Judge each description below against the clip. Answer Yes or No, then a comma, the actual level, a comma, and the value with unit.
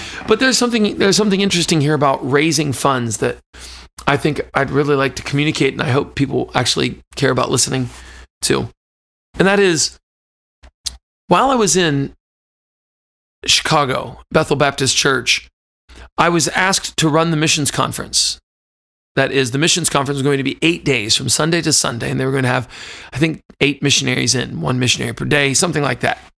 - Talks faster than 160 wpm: Yes, average, 180 wpm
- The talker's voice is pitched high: No, medium, 140 Hz